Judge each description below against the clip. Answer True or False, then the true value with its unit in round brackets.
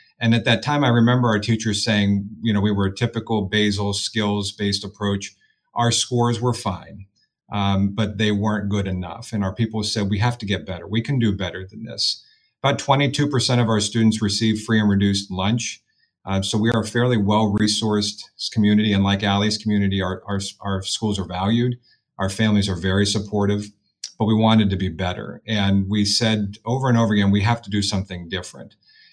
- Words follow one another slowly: False (200 wpm)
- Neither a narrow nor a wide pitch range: False (2.3 semitones)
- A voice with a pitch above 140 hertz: False (105 Hz)